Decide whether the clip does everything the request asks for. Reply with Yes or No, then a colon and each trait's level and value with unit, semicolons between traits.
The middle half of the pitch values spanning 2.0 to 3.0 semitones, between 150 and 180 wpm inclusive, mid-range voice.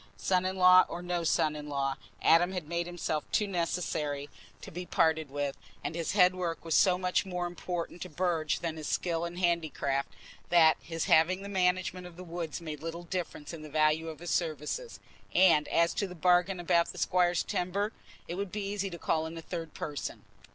No: narrow, 2.4 semitones; average, 200 wpm; medium, 170 Hz